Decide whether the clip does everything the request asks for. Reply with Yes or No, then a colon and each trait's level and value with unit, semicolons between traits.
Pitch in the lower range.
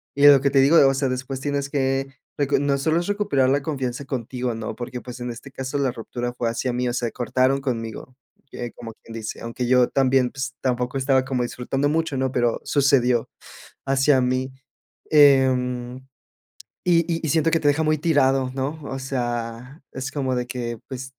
Yes: low, 130 Hz